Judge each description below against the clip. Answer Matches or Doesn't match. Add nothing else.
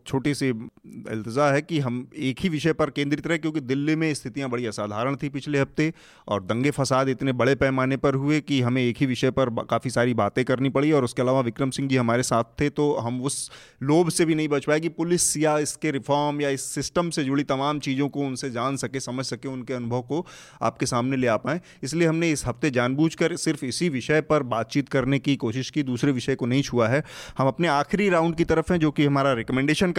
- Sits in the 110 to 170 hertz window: Matches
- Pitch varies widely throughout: Doesn't match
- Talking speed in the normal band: Doesn't match